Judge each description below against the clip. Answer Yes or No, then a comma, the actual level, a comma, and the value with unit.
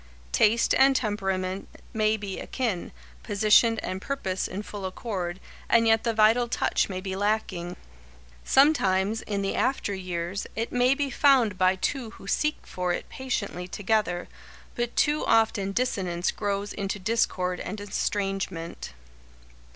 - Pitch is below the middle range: No, high, 205 Hz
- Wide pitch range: No, average, 3.5 semitones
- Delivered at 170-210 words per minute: No, average, 140 wpm